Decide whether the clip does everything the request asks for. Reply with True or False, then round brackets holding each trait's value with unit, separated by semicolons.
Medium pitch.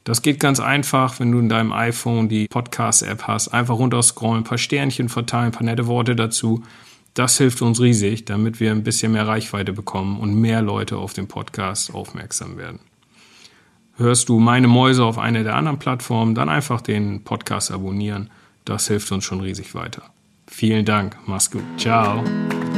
False (115 Hz)